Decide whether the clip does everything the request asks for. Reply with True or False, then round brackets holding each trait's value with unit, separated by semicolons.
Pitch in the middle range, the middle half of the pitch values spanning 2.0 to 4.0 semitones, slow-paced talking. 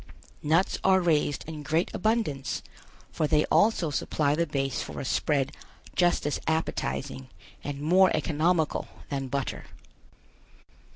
True (155 Hz; 3.6 semitones; 125 wpm)